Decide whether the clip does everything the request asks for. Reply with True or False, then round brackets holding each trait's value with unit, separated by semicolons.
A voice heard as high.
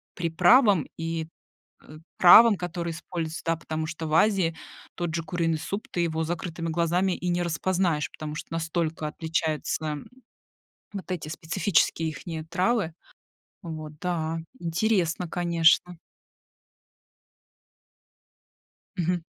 False (165 Hz)